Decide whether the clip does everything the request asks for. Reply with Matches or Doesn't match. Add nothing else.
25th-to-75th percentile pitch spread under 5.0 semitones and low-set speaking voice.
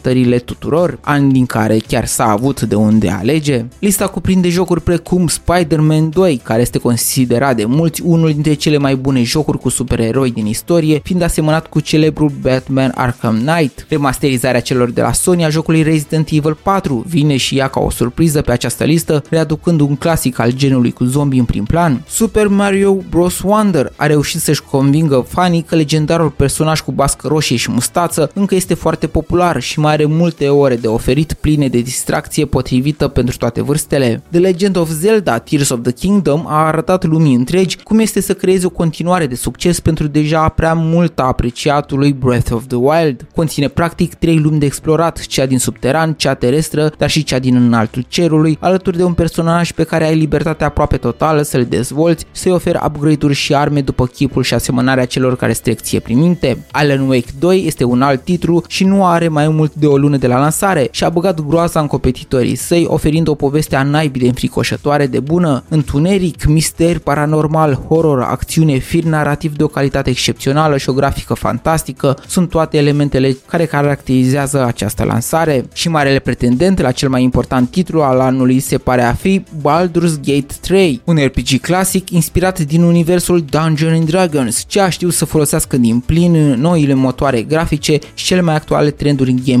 Doesn't match